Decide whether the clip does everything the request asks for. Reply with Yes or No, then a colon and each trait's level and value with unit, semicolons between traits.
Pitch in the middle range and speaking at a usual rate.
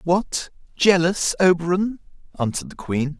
No: medium, 175 Hz; slow, 115 wpm